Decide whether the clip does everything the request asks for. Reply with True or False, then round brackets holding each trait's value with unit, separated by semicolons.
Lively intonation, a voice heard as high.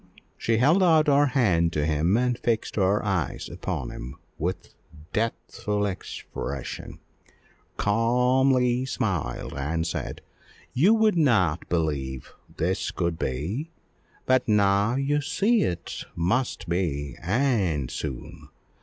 False (7.6 semitones; 105 Hz)